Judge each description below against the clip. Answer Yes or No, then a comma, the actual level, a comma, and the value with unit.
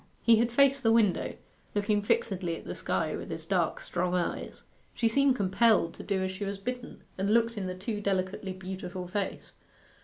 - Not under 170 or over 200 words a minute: Yes, average, 190 wpm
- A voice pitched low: No, high, 200 Hz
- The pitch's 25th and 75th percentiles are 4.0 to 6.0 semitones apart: No, average, 3.6 semitones